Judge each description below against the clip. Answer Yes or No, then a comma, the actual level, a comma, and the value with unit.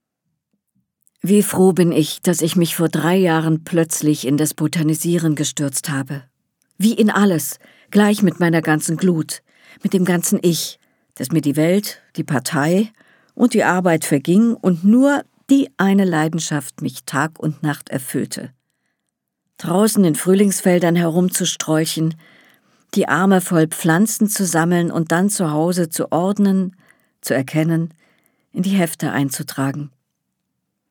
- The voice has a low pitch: No, medium, 170 Hz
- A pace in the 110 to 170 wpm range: Yes, average, 135 wpm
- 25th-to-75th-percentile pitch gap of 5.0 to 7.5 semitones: No, average, 3.7 semitones